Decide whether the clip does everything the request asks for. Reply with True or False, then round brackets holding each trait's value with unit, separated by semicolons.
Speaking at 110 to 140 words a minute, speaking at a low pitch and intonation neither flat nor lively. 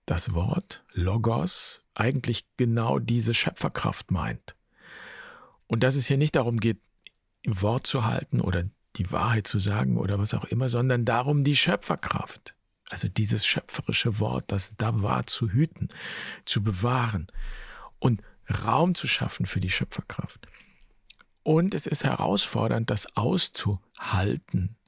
True (135 wpm; 115 Hz; 3.8 semitones)